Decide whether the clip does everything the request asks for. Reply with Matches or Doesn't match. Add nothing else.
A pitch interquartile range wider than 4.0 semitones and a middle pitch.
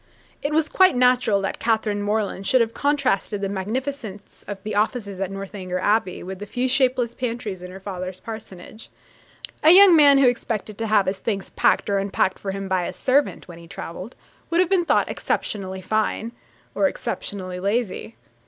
Doesn't match